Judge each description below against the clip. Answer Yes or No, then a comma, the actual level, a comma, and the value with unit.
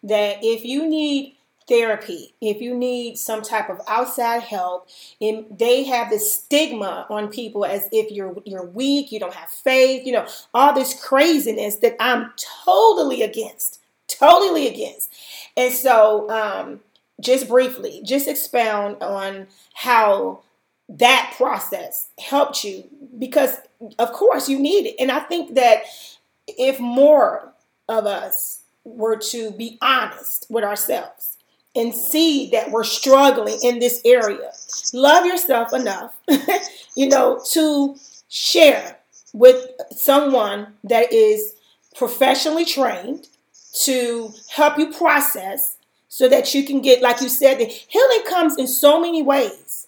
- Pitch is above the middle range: Yes, very high, 265 Hz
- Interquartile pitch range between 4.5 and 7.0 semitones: Yes, average, 4.8 semitones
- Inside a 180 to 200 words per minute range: No, slow, 135 wpm